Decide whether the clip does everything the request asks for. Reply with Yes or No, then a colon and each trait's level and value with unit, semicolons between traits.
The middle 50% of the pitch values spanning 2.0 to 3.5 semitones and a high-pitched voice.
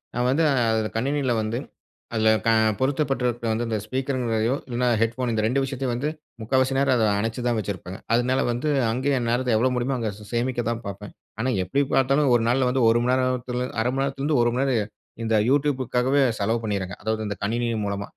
No: average, 2.8 semitones; low, 120 Hz